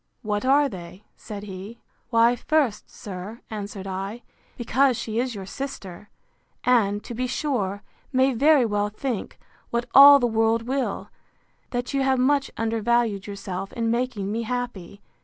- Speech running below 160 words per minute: Yes, average, 150 wpm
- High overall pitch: Yes, high, 230 Hz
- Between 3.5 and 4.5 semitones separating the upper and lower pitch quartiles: Yes, average, 3.9 semitones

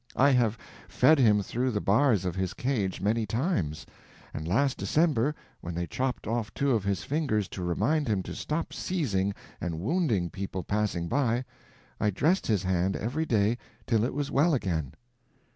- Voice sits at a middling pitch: No, low, 110 Hz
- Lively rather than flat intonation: Yes, wide, 6.4 semitones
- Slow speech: No, average, 175 wpm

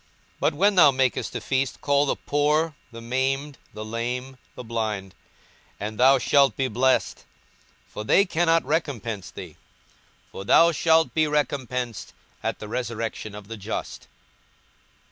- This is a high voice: No, low, 130 Hz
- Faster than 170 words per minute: No, average, 150 wpm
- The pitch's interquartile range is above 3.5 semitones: Yes, average, 4.5 semitones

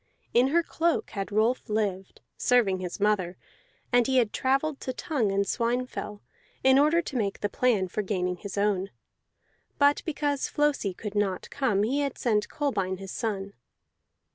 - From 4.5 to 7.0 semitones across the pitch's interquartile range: Yes, average, 5.2 semitones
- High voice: Yes, high, 220 Hz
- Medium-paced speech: Yes, average, 165 wpm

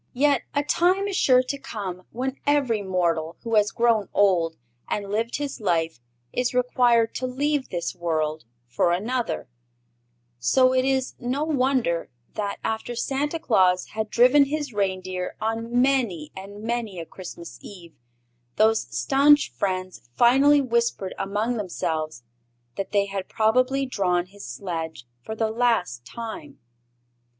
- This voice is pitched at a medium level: No, high, 220 Hz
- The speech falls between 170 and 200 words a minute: No, average, 140 wpm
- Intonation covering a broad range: Yes, wide, 5.8 semitones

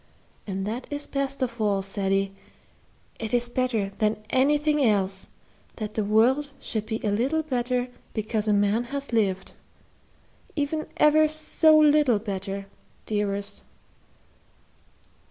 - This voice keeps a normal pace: No, slow, 125 wpm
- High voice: Yes, high, 225 Hz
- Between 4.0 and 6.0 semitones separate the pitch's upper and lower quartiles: Yes, wide, 5.4 semitones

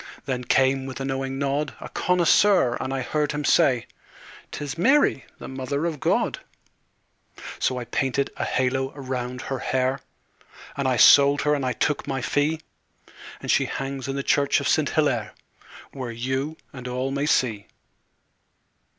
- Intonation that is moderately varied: No, narrow, 2.0 semitones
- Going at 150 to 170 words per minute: Yes, average, 160 wpm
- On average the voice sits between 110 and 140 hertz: Yes, low, 135 Hz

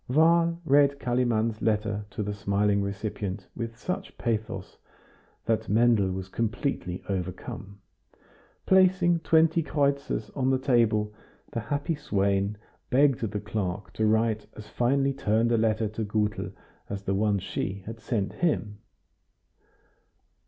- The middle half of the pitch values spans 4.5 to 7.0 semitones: Yes, average, 4.9 semitones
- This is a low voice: Yes, low, 110 Hz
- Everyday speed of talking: No, slow, 130 wpm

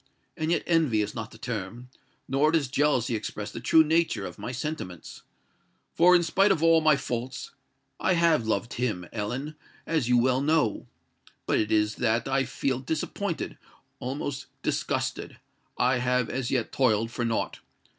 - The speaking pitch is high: No, low, 125 Hz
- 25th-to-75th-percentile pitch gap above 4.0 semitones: Yes, average, 5.1 semitones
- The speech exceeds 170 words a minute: No, average, 150 wpm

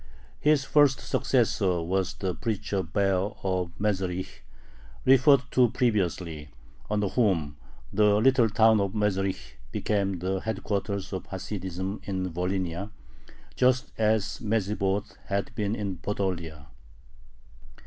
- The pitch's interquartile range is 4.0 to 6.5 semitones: No, narrow, 2.6 semitones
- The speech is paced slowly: Yes, slow, 110 wpm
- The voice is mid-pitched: No, low, 100 Hz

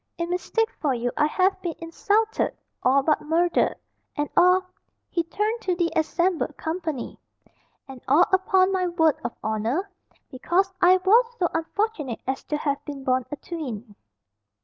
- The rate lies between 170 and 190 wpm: No, average, 155 wpm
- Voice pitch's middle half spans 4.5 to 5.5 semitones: Yes, average, 4.8 semitones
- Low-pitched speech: No, very high, 335 Hz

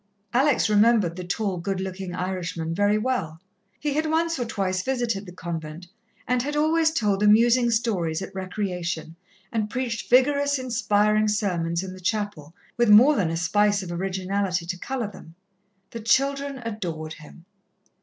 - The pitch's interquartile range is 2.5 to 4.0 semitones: No, average, 5.1 semitones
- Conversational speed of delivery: Yes, average, 155 wpm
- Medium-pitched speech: No, high, 205 Hz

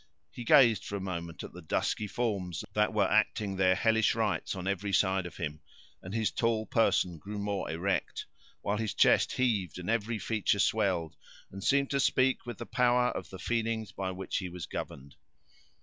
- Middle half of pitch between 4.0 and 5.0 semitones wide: No, average, 3.5 semitones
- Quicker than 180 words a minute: Yes, average, 190 wpm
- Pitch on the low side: Yes, low, 100 Hz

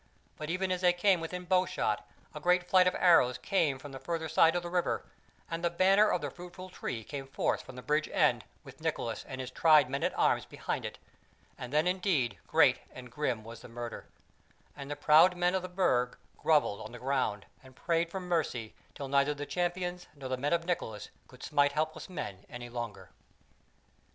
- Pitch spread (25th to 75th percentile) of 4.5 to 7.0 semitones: Yes, wide, 5.6 semitones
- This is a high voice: No, medium, 150 Hz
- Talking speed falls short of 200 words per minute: No, fast, 205 wpm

